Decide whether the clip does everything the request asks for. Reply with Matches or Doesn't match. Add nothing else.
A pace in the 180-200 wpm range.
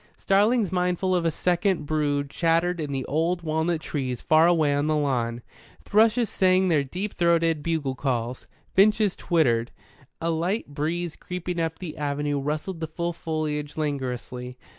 Doesn't match